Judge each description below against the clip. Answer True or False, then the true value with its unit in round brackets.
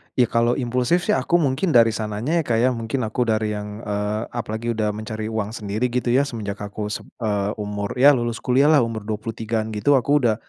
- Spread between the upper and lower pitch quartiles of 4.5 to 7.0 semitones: False (2.9 semitones)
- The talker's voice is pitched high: False (115 Hz)